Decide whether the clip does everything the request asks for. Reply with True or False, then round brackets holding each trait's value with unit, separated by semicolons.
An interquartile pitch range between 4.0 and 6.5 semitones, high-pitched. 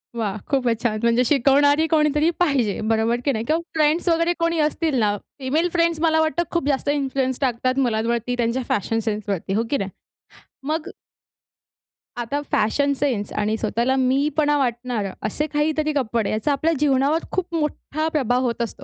True (4.6 semitones; 270 Hz)